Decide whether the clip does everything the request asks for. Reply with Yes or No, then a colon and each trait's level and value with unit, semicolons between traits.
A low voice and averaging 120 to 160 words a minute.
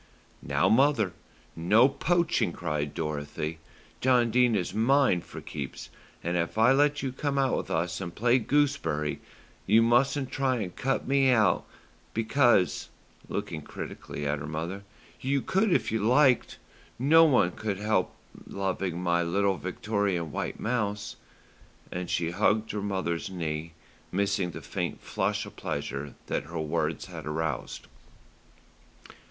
Yes: low, 100 Hz; average, 140 wpm